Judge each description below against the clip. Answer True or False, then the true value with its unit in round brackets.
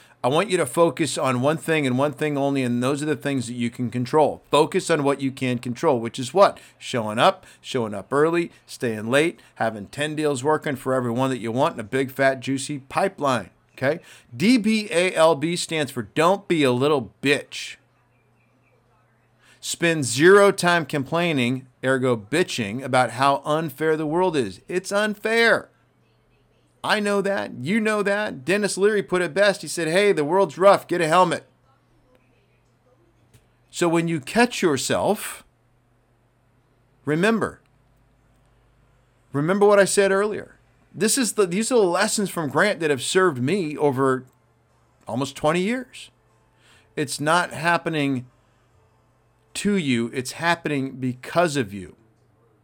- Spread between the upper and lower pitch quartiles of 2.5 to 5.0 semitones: False (5.6 semitones)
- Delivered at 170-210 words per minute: False (150 wpm)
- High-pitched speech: False (140 Hz)